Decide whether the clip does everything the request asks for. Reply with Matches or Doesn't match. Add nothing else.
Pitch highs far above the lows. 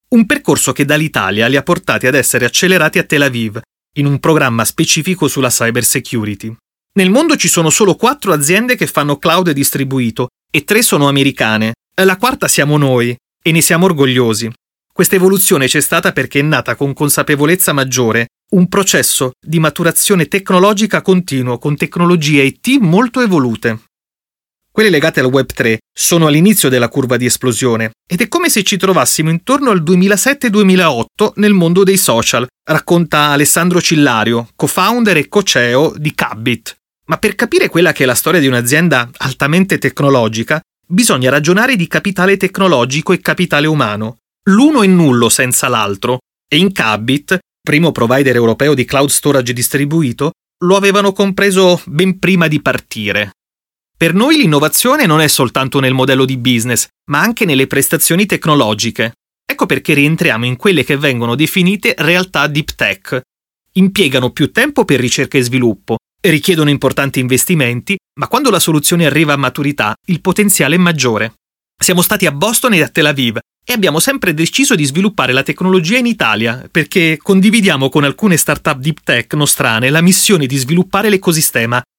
Matches